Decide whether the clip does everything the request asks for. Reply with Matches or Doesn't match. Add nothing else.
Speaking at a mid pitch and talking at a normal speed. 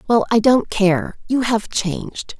Doesn't match